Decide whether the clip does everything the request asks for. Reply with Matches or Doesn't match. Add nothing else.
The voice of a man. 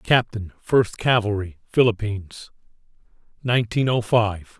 Matches